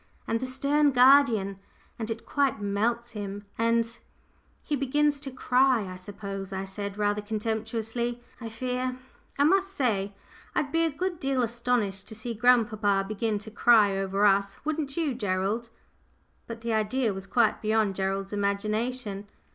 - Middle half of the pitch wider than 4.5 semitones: No, average, 4.0 semitones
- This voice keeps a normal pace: Yes, average, 155 wpm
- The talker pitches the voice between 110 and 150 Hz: No, high, 225 Hz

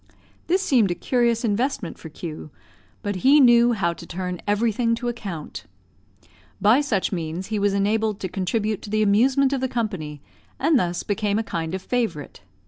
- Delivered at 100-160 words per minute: No, average, 175 wpm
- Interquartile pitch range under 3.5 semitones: No, average, 4.6 semitones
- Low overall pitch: No, high, 210 Hz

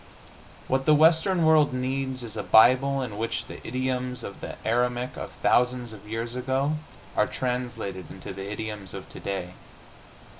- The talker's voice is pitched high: No, low, 125 Hz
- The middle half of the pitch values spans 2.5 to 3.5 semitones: Yes, average, 3.2 semitones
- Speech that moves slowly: No, average, 155 wpm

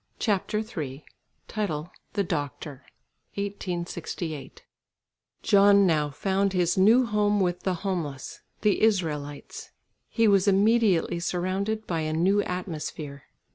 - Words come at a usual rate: No, slow, 105 wpm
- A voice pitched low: No, medium, 185 Hz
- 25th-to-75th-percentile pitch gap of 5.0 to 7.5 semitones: No, average, 4.3 semitones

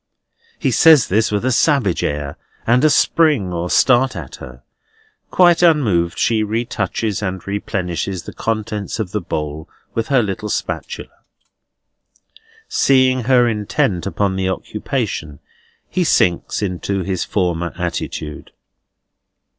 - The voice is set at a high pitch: No, low, 105 Hz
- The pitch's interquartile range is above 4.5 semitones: Yes, wide, 5.4 semitones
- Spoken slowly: Yes, slow, 125 wpm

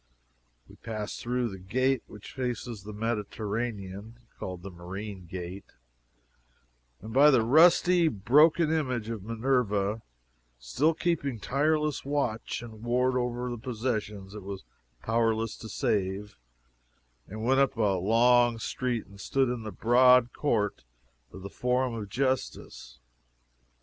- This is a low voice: Yes, low, 115 Hz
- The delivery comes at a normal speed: No, slow, 130 wpm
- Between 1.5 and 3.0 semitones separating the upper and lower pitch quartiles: No, average, 3.7 semitones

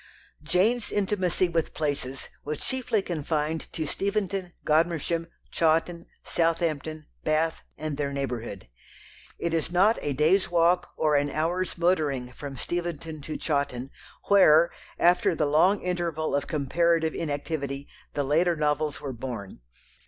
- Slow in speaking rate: Yes, slow, 130 wpm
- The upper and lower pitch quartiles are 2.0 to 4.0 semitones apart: Yes, average, 3.2 semitones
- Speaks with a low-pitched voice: No, medium, 160 Hz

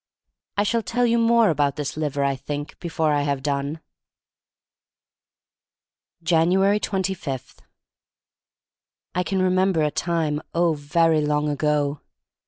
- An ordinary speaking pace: No, slow, 125 wpm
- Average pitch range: Yes, average, 4.2 semitones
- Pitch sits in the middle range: Yes, medium, 160 Hz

